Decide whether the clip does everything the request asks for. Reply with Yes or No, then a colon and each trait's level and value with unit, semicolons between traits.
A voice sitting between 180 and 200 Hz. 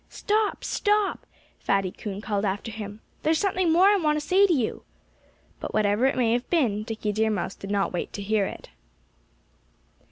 No: high, 225 Hz